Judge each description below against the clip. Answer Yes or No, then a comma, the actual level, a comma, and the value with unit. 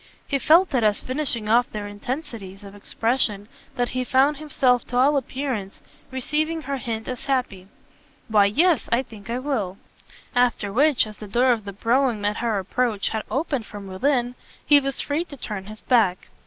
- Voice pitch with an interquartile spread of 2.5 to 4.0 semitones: No, average, 4.6 semitones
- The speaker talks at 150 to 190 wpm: Yes, average, 180 wpm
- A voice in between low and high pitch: No, high, 245 Hz